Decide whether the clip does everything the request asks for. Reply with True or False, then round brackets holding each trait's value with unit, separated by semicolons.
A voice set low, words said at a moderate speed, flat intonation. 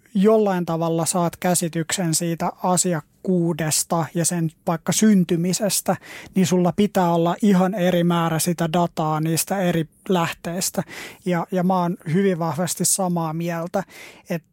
False (175 Hz; 130 wpm; 1.8 semitones)